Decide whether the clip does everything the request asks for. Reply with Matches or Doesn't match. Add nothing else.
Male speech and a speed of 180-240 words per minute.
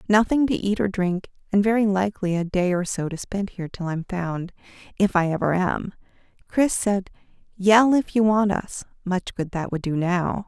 Doesn't match